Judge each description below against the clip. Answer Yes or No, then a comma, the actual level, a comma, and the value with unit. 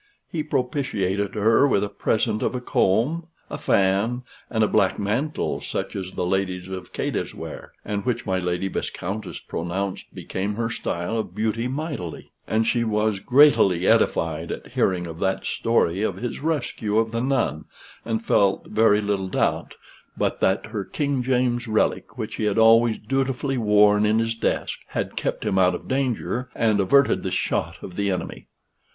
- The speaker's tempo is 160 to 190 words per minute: Yes, average, 170 wpm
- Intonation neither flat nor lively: Yes, average, 4.1 semitones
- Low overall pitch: Yes, low, 110 Hz